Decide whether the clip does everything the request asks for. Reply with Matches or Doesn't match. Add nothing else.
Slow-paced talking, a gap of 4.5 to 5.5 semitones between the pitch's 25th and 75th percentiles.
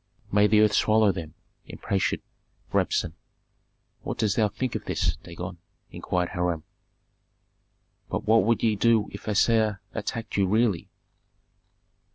Doesn't match